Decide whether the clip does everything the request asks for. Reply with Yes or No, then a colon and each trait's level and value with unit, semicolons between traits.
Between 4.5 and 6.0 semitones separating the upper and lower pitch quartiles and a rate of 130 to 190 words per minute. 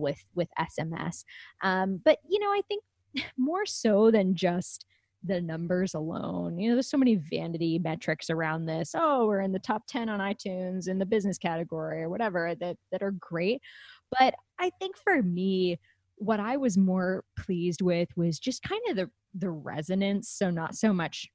Yes: average, 5.1 semitones; average, 185 wpm